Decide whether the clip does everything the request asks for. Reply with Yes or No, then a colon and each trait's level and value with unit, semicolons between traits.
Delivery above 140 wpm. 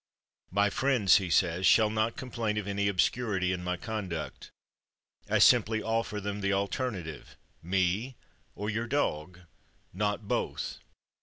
No: slow, 135 wpm